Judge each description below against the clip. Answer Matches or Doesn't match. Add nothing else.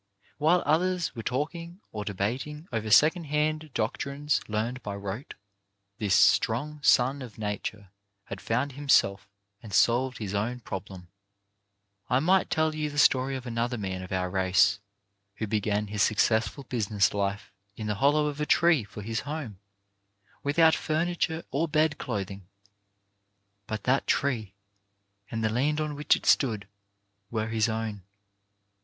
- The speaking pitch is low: Matches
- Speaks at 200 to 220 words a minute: Doesn't match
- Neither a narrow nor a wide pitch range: Doesn't match